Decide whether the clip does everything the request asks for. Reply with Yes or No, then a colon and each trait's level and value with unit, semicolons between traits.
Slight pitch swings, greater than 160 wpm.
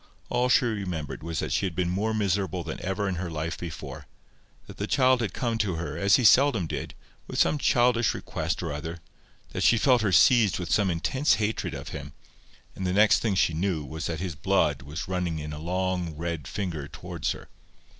No: average, 4.7 semitones; fast, 205 wpm